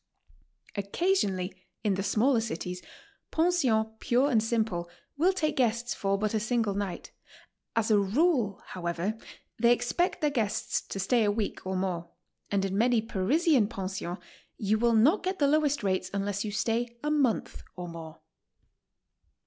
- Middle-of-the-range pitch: No, high, 220 Hz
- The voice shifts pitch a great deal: No, average, 4.4 semitones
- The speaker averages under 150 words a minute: No, average, 155 wpm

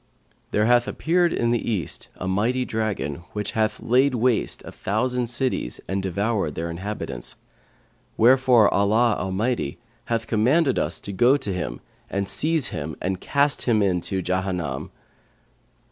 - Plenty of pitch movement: No, average, 4.8 semitones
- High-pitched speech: No, low, 110 Hz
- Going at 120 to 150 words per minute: Yes, average, 145 wpm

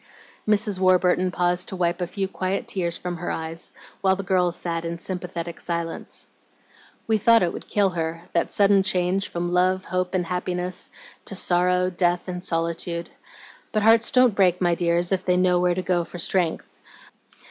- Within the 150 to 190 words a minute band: Yes, average, 180 wpm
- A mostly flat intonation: Yes, narrow, 1.5 semitones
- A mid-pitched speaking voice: Yes, medium, 180 Hz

